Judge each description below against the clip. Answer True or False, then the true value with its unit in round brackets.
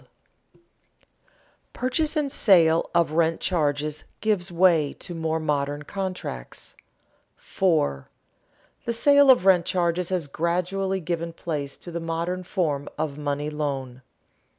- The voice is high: False (170 Hz)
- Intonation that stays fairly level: False (3.7 semitones)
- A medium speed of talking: False (125 wpm)